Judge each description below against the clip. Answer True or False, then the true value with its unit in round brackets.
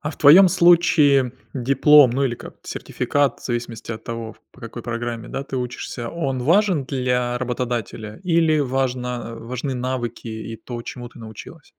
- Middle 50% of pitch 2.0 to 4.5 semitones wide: True (3.1 semitones)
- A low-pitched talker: True (125 Hz)